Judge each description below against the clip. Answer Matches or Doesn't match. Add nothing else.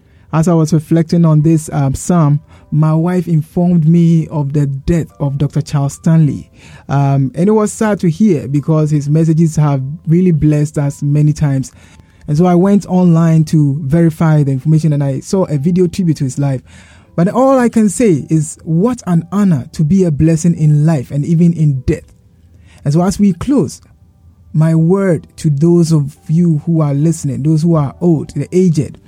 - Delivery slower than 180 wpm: Doesn't match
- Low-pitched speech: Doesn't match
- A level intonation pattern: Doesn't match